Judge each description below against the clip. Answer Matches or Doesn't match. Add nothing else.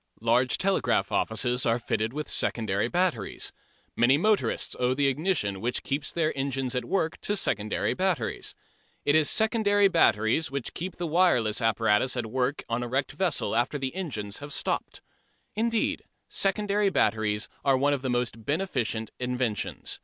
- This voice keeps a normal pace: Matches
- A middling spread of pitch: Doesn't match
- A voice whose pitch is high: Doesn't match